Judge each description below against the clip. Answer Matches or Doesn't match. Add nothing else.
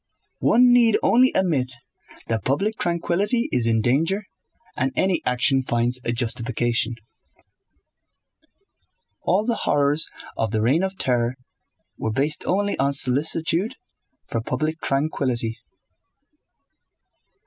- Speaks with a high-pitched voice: Doesn't match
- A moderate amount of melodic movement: Doesn't match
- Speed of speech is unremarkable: Doesn't match